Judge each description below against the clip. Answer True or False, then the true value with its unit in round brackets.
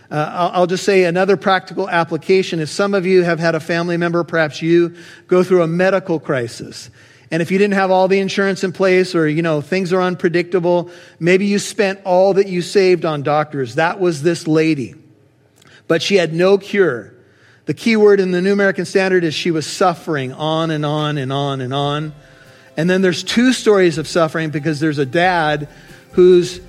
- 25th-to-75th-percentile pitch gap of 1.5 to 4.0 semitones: True (3.3 semitones)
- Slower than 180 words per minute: False (200 wpm)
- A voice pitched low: False (170 Hz)